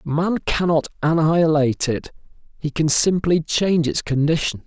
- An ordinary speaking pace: No, slow, 130 wpm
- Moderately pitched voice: Yes, medium, 155 Hz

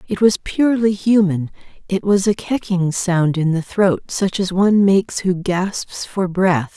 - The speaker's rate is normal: Yes, average, 180 wpm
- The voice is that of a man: No, female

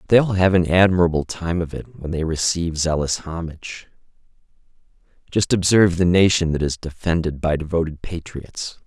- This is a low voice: Yes, very low, 85 Hz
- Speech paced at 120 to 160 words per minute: Yes, average, 155 wpm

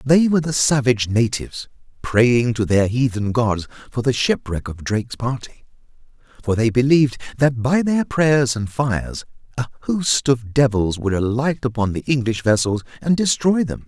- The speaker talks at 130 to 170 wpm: Yes, average, 165 wpm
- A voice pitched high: No, low, 125 Hz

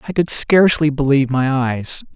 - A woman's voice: No, male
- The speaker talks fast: No, average, 165 wpm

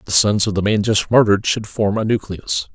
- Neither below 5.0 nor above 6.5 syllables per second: Yes, 5.5 syllables/s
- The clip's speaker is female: No, male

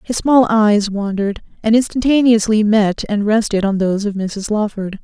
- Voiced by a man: No, female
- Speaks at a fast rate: No, average, 165 wpm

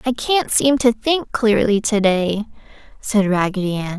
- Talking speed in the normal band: Yes, average, 165 wpm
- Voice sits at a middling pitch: No, high, 220 Hz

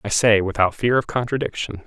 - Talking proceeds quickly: No, average, 195 wpm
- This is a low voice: Yes, low, 110 Hz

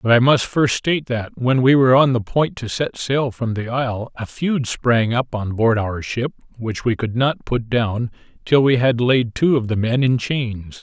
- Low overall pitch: Yes, low, 120 Hz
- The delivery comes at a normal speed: No, fast, 235 wpm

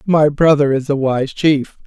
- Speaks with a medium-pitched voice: Yes, medium, 145 Hz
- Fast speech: No, average, 195 wpm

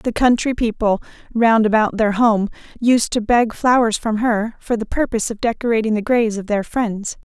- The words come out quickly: No, average, 190 wpm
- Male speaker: No, female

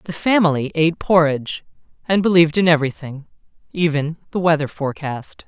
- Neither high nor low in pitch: Yes, medium, 155 Hz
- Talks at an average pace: No, slow, 130 wpm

